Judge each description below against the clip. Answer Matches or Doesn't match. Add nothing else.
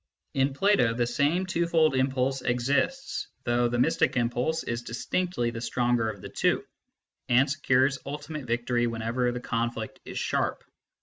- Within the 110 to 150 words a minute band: Matches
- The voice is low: Matches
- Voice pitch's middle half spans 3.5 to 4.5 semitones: Doesn't match